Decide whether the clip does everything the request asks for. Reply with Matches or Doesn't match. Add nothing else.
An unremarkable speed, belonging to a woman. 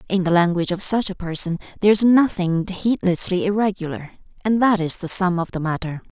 Matches